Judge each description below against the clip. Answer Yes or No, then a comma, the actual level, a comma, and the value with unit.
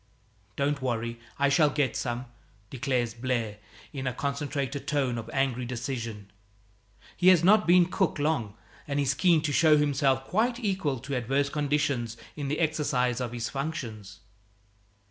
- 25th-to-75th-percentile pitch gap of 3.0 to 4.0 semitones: Yes, average, 3.5 semitones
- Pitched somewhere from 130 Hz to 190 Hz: Yes, medium, 140 Hz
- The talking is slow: No, average, 150 wpm